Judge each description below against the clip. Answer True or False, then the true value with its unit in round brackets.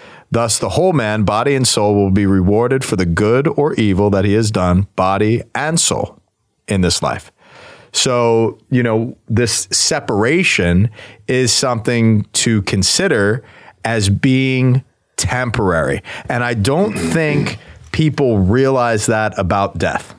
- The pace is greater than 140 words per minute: False (135 wpm)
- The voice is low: True (110 Hz)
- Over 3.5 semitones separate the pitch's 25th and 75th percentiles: True (4.2 semitones)